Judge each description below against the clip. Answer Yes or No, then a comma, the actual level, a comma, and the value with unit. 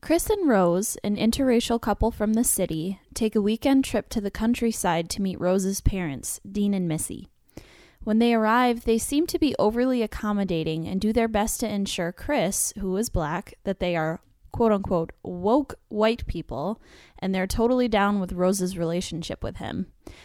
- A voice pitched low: No, high, 205 Hz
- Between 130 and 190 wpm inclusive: Yes, average, 175 wpm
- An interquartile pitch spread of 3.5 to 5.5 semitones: Yes, average, 4.1 semitones